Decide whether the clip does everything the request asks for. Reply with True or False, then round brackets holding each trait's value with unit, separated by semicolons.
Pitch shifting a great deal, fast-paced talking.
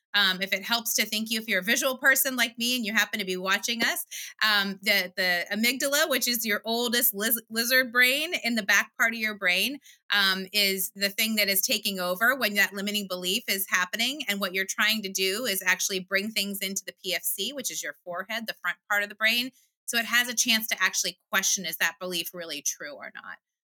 False (3.5 semitones; 230 wpm)